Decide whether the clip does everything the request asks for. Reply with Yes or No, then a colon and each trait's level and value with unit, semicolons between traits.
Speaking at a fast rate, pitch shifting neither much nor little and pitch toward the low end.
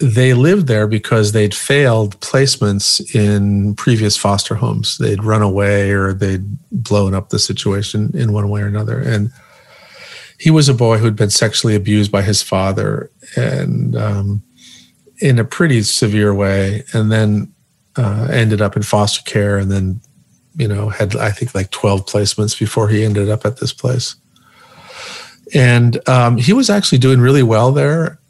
No: average, 165 wpm; average, 3.8 semitones; low, 110 Hz